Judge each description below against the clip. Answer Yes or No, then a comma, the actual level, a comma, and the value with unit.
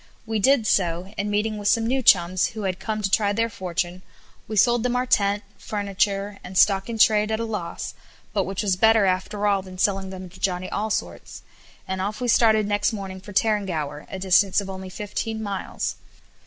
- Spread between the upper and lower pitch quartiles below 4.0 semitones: Yes, narrow, 2.4 semitones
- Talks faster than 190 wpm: Yes, average, 200 wpm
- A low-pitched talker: No, high, 200 Hz